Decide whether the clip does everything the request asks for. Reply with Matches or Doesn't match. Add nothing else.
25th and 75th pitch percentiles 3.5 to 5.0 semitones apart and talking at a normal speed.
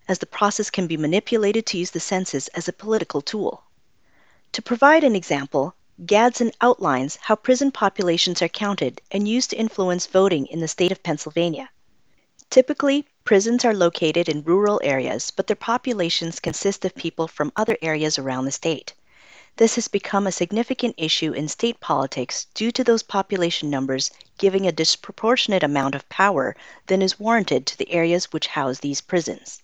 Doesn't match